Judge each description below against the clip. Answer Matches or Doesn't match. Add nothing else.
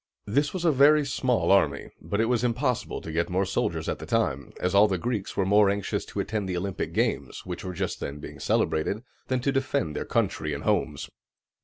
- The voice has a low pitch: Matches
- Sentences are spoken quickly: Matches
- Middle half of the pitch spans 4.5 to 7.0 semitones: Matches